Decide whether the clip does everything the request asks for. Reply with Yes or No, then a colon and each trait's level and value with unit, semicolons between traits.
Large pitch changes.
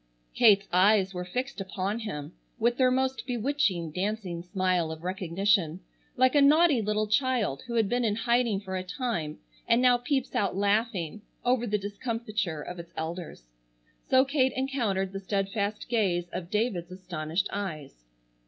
No: average, 4.9 semitones